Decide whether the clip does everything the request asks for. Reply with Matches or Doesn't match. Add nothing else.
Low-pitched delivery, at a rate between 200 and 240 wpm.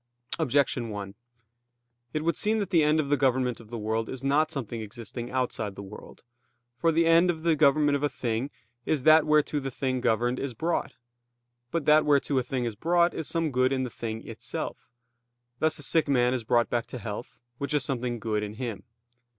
Matches